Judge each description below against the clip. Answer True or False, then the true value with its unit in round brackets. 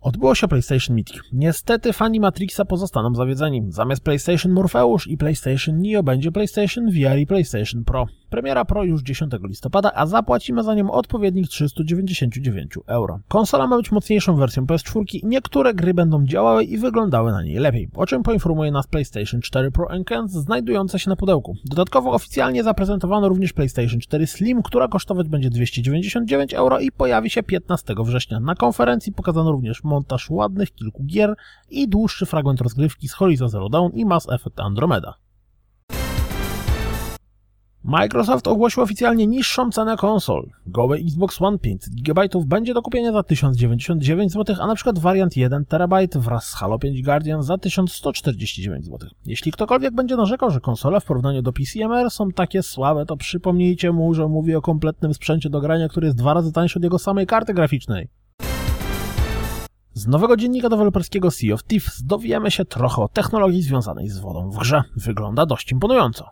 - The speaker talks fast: True (165 wpm)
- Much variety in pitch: True (7.8 semitones)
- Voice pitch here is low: False (155 Hz)